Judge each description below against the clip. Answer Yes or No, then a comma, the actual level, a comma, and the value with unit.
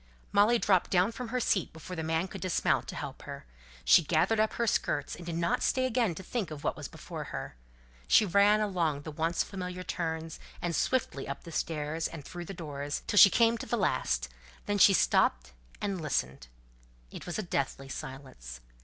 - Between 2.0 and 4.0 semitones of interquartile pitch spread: No, average, 5.3 semitones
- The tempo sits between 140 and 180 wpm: No, average, 200 wpm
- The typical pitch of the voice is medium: Yes, medium, 170 Hz